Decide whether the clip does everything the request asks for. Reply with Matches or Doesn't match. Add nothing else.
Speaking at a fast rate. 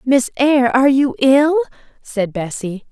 Doesn't match